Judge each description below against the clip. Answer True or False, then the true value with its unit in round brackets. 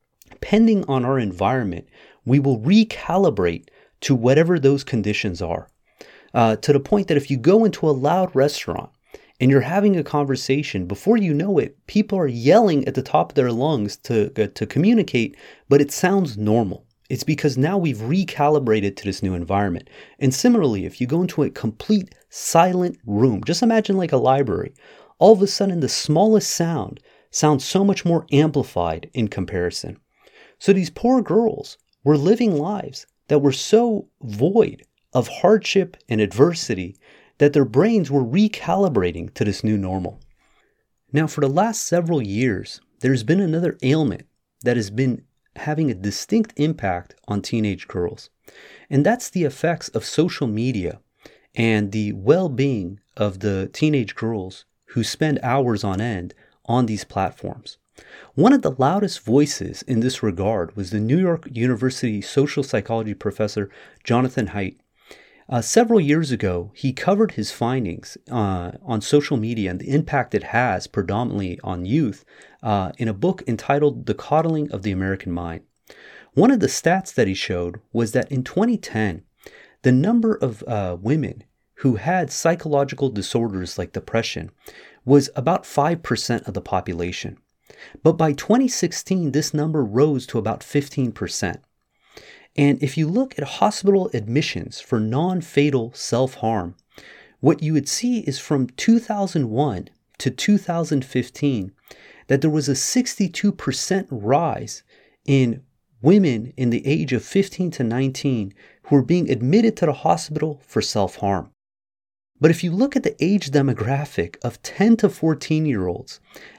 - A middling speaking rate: True (155 wpm)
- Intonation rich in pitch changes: True (7.3 semitones)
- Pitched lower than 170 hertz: True (135 Hz)